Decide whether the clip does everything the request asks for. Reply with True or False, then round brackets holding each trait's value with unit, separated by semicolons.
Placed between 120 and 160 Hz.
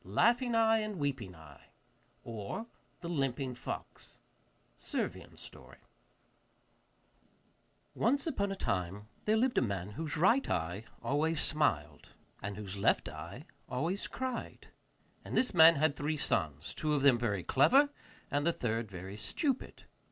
True (140 Hz)